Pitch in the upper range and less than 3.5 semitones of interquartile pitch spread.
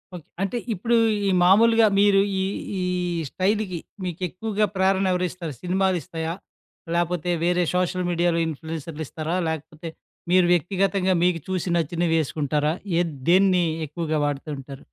No: medium, 175 Hz; average, 2.7 semitones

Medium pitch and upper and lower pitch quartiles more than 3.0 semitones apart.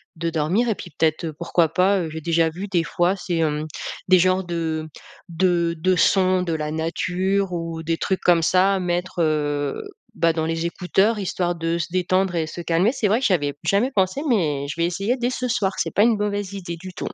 No: medium, 175 Hz; average, 2.7 semitones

